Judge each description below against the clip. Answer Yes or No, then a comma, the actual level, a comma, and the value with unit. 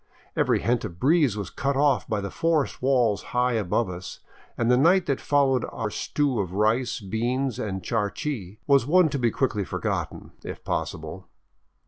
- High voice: No, low, 120 Hz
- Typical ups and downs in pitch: Yes, average, 5.0 semitones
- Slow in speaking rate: No, average, 175 wpm